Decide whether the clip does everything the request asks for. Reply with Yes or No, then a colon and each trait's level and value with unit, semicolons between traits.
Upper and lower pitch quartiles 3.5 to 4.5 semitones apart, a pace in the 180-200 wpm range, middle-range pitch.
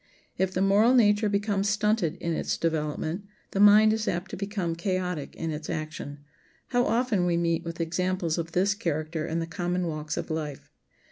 Yes: average, 3.9 semitones; average, 185 wpm; medium, 180 Hz